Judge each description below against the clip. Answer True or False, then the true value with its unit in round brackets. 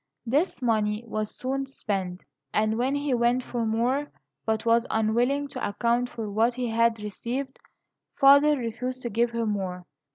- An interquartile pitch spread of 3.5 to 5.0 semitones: False (2.8 semitones)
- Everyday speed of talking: True (160 wpm)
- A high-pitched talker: True (235 Hz)